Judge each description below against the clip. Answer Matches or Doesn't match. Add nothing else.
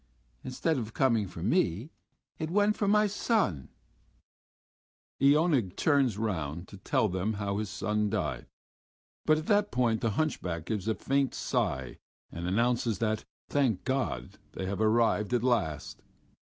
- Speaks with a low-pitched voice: Matches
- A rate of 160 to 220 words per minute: Doesn't match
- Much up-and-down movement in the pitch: Matches